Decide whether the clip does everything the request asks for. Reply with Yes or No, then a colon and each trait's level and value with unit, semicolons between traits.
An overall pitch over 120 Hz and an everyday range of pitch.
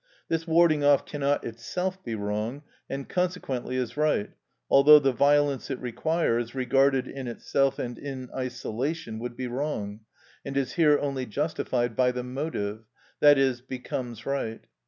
Yes: low, 135 Hz; average, 3.2 semitones